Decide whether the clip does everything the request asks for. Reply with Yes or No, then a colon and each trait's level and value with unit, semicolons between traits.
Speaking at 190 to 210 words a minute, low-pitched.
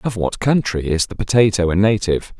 Yes: average, 200 wpm; low, 100 Hz